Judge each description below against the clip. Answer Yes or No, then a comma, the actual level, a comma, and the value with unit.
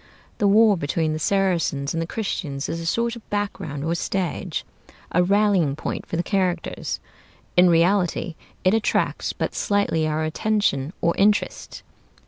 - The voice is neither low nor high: Yes, medium, 180 Hz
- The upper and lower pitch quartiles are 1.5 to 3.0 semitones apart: No, average, 4.1 semitones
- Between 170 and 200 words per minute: No, average, 150 wpm